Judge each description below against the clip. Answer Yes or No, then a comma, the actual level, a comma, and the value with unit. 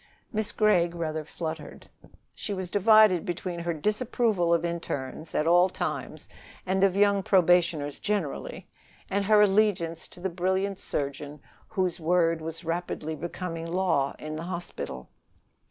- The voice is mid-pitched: Yes, medium, 175 Hz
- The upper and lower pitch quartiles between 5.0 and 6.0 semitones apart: No, average, 3.0 semitones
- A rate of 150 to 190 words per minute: No, average, 140 wpm